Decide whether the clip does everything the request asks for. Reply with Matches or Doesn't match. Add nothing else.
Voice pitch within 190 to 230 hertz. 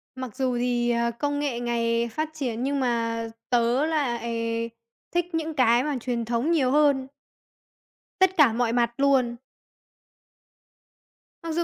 Doesn't match